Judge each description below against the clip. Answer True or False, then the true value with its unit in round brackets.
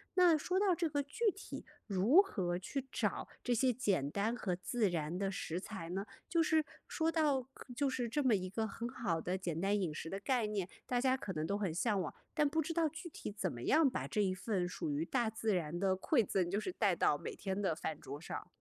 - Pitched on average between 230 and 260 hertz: False (210 Hz)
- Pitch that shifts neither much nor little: False (7.0 semitones)